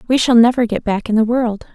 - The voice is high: Yes, high, 230 Hz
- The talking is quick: Yes, fast, 275 wpm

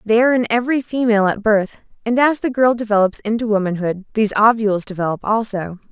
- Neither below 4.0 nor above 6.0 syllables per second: No, 6.4 syllables/s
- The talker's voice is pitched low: No, high, 220 Hz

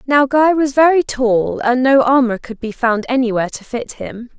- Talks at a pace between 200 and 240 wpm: Yes, fast, 205 wpm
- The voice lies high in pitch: Yes, very high, 255 Hz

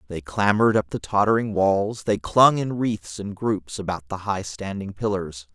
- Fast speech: No, average, 185 wpm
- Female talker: No, male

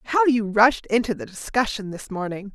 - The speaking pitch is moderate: No, high, 225 Hz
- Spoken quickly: No, average, 190 wpm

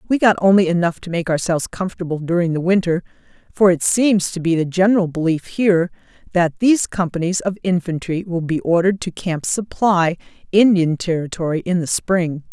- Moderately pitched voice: Yes, medium, 180 Hz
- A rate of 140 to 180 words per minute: Yes, average, 175 wpm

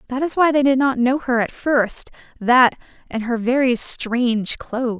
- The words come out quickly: No, average, 190 wpm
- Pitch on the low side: No, very high, 250 Hz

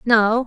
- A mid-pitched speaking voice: No, high, 230 Hz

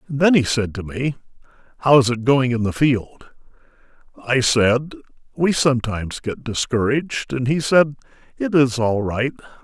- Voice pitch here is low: Yes, low, 130 Hz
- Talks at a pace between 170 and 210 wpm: No, average, 155 wpm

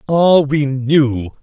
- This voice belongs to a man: Yes, male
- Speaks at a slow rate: Yes, slow, 125 wpm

